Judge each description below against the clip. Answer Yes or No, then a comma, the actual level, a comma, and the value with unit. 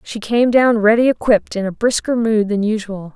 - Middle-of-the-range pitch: No, high, 220 Hz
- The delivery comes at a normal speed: No, fast, 210 wpm